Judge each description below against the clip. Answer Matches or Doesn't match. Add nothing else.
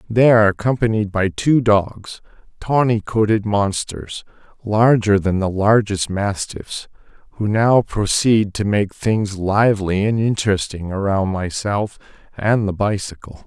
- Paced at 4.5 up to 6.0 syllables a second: Doesn't match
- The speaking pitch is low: Matches